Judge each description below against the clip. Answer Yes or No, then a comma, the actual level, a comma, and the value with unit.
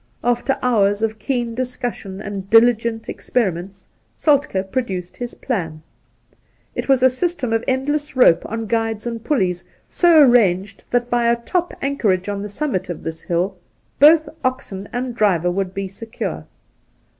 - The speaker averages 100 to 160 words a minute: Yes, average, 155 wpm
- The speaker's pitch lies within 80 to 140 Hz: No, high, 225 Hz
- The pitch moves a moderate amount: Yes, average, 4.6 semitones